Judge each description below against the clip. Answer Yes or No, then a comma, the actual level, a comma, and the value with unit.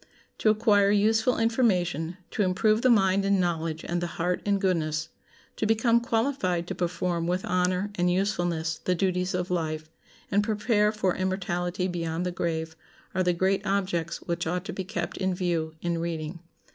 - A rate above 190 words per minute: No, average, 170 wpm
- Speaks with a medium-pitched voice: Yes, medium, 180 Hz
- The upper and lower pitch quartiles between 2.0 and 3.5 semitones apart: Yes, average, 2.9 semitones